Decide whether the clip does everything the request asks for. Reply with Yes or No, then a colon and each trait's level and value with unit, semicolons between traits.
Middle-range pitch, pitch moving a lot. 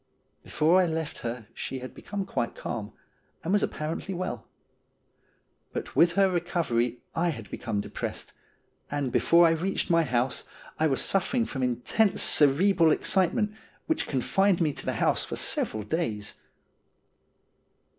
Yes: medium, 160 Hz; wide, 6.6 semitones